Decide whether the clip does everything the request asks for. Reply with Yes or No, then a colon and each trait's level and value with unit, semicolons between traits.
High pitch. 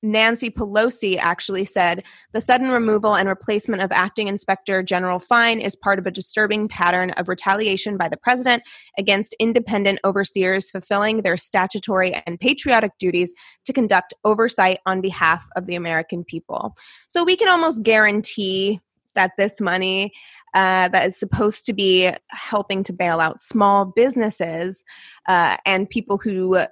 Yes: high, 195 Hz